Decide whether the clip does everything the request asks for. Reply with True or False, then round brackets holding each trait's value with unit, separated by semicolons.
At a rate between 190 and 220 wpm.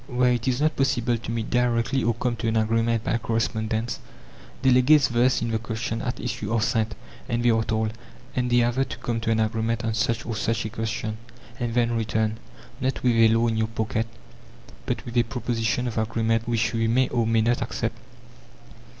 True (200 wpm)